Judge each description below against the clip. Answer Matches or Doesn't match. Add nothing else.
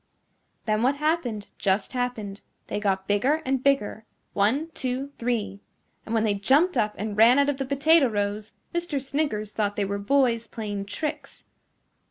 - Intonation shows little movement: Doesn't match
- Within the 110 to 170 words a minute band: Matches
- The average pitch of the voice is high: Matches